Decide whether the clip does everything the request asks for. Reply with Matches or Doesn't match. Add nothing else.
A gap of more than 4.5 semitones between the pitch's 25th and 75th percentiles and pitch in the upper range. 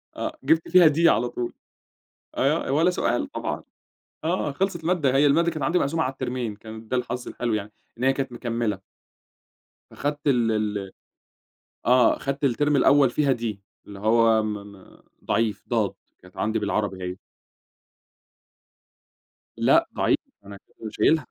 Doesn't match